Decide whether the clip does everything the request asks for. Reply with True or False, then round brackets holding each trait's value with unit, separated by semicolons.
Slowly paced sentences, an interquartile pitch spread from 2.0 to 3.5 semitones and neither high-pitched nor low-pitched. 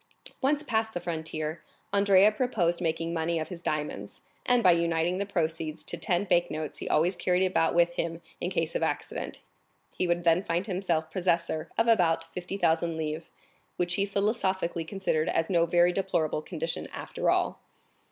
False (170 wpm; 2.7 semitones; 175 Hz)